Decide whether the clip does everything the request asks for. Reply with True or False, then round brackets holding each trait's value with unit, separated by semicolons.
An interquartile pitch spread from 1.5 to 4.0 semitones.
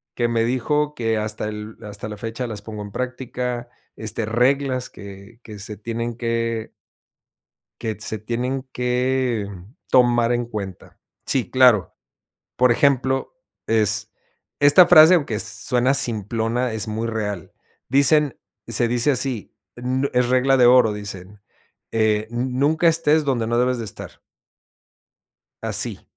True (2.8 semitones)